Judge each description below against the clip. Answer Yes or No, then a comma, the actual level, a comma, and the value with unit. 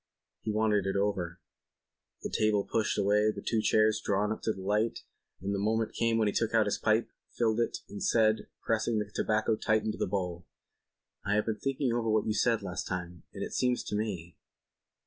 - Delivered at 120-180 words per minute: No, fast, 205 wpm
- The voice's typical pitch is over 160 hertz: No, low, 110 Hz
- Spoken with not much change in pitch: Yes, narrow, 1.8 semitones